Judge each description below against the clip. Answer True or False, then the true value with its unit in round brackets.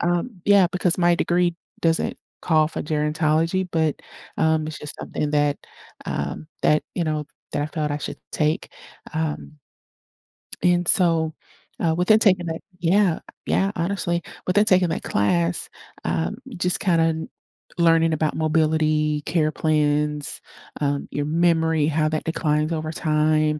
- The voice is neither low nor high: True (160 Hz)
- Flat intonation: True (2.2 semitones)